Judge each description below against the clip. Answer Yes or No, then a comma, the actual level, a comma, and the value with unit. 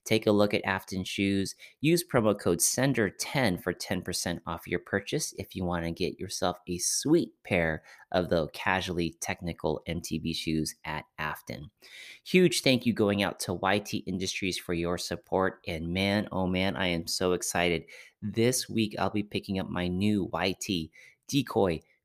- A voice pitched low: Yes, very low, 95 Hz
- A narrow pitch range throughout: No, average, 3.0 semitones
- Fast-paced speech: No, average, 165 wpm